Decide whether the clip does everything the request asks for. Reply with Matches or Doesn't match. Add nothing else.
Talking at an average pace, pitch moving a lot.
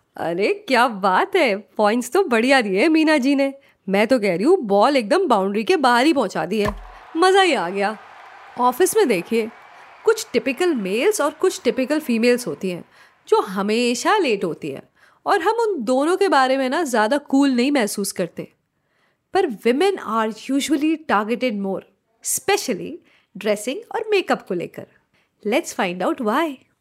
Matches